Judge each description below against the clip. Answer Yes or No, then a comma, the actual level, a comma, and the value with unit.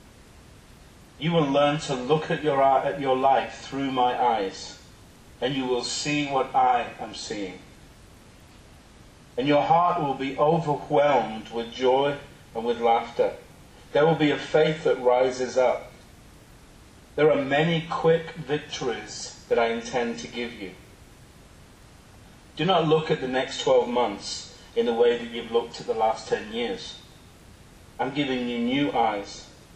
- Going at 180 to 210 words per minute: No, average, 150 wpm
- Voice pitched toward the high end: No, medium, 140 Hz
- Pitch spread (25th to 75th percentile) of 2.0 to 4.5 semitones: Yes, average, 4.2 semitones